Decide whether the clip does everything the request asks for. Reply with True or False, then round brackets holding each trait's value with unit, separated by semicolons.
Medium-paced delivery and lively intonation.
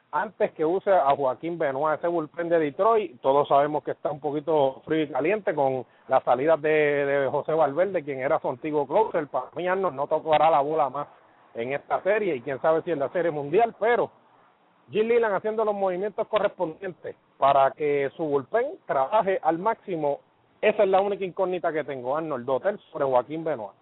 False (190 wpm; 4.9 semitones)